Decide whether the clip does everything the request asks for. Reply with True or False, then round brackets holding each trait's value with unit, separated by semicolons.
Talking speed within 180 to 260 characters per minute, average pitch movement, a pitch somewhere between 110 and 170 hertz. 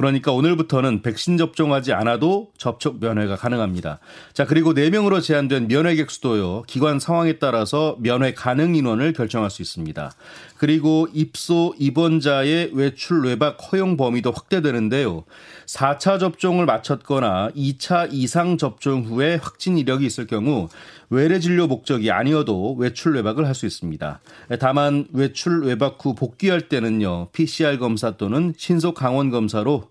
False (330 characters per minute; 5.0 semitones; 140 Hz)